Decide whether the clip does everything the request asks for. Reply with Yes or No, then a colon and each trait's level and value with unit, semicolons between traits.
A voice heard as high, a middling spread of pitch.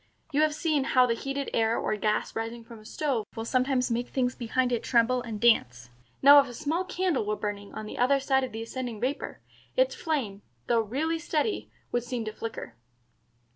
Yes: high, 245 Hz; average, 3.8 semitones